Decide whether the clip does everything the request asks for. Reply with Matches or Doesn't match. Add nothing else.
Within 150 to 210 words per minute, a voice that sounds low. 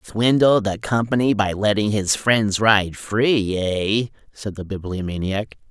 Doesn't match